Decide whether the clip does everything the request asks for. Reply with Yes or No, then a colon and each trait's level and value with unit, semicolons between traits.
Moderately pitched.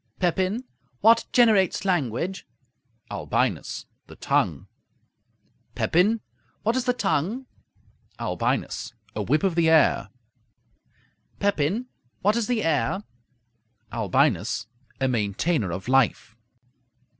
Yes: medium, 175 Hz